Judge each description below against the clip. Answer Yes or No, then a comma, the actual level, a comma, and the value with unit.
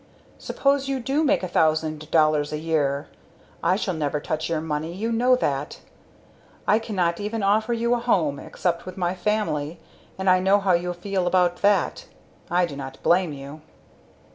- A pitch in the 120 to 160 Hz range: No, medium, 175 Hz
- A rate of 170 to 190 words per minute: Yes, average, 175 wpm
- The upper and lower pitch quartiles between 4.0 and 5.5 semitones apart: Yes, average, 5.1 semitones